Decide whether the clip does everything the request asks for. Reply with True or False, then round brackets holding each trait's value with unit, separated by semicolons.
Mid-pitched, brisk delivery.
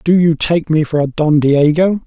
True (160 Hz; 235 wpm)